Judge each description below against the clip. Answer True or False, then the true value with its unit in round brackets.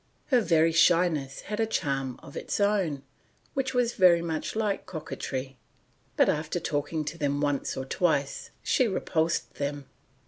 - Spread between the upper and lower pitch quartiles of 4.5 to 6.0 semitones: True (5.2 semitones)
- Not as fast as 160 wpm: True (150 wpm)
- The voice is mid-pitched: True (160 Hz)